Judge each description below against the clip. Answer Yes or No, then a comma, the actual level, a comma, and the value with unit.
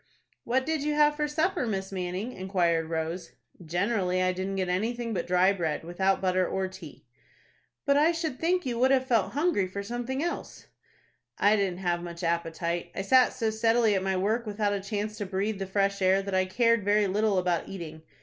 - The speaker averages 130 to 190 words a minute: No, average, 200 wpm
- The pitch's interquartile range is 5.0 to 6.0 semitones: No, average, 4.4 semitones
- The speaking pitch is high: Yes, high, 195 Hz